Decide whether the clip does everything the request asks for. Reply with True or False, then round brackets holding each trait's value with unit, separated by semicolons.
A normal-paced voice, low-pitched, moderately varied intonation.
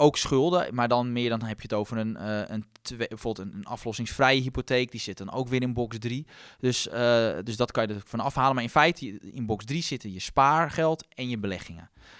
False (220 wpm; 120 Hz; 3.1 semitones)